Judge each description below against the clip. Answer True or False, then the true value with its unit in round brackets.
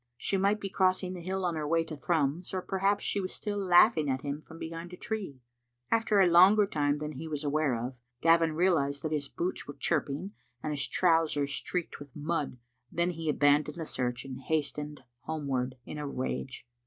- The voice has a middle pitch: True (160 Hz)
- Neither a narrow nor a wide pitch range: True (4.1 semitones)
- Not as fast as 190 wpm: False (200 wpm)